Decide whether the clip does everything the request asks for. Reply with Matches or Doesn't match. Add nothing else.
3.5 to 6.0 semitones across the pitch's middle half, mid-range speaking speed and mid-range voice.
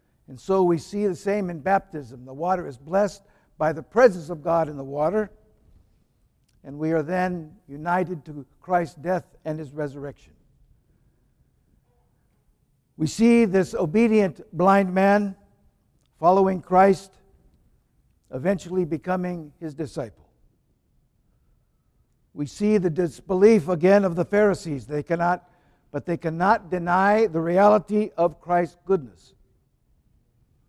Doesn't match